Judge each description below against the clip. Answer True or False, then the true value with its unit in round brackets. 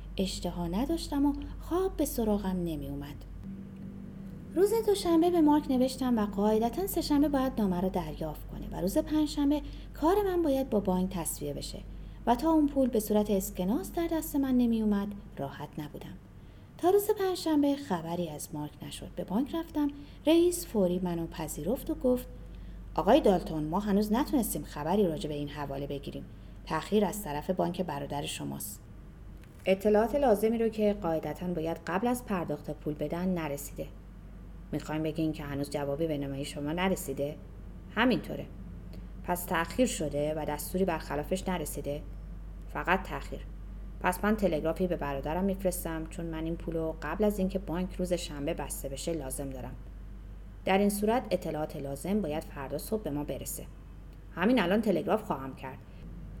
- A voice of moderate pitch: True (180 Hz)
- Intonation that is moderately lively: False (7.4 semitones)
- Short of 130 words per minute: False (155 wpm)